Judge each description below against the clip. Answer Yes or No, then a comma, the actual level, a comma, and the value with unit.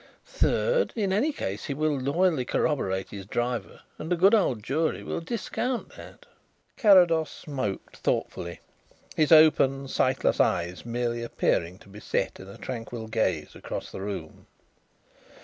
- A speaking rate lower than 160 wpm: Yes, average, 145 wpm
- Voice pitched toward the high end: No, low, 130 Hz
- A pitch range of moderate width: No, wide, 8.0 semitones